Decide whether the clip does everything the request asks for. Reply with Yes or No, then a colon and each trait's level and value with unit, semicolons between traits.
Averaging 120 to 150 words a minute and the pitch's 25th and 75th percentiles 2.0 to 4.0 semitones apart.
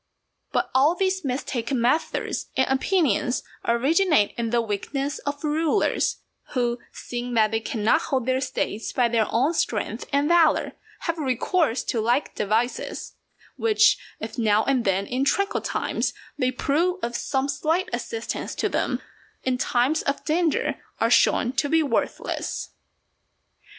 No: average, 145 wpm; average, 4.8 semitones